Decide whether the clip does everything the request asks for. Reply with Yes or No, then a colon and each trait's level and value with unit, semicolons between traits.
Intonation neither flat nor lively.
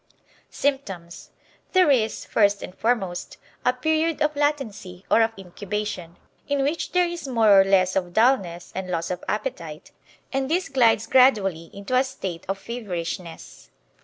No: wide, 6.6 semitones